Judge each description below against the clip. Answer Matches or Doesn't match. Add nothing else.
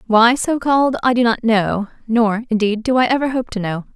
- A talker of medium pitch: Doesn't match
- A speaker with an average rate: Doesn't match